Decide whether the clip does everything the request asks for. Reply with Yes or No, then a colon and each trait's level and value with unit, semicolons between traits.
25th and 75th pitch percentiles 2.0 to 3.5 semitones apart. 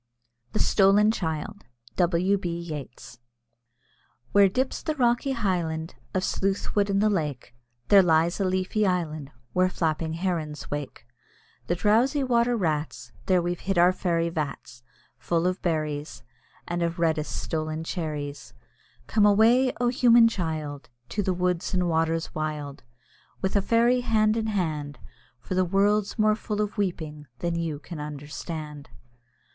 No: average, 4.7 semitones